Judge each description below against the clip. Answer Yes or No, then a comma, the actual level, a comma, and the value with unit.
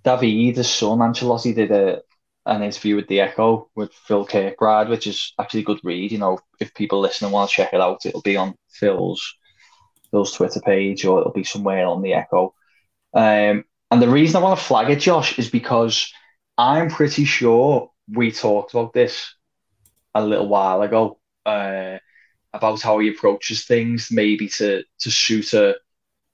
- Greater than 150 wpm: Yes, average, 180 wpm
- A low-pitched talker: Yes, low, 110 Hz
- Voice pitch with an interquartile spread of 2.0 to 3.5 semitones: Yes, average, 2.7 semitones